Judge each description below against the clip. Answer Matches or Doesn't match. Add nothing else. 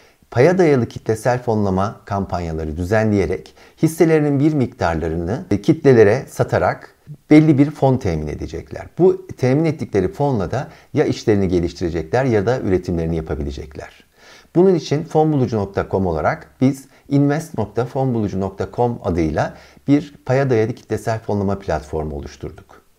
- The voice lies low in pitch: Matches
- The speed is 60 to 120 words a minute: Matches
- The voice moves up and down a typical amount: Doesn't match